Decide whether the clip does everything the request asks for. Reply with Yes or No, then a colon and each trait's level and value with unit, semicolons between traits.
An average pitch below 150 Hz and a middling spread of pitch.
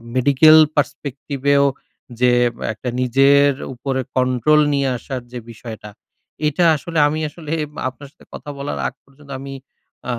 No: medium, 140 Hz; narrow, 2.3 semitones